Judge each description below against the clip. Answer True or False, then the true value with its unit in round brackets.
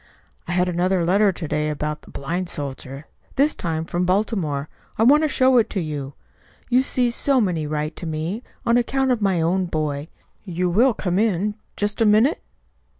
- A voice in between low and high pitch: True (180 Hz)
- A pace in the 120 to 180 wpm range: False (190 wpm)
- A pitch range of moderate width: False (6.1 semitones)